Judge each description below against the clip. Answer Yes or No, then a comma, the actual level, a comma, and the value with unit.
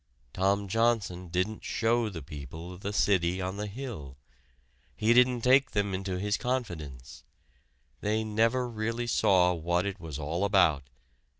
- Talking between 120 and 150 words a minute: Yes, average, 140 wpm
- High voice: No, low, 100 Hz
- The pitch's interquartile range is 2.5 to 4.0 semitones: No, average, 4.4 semitones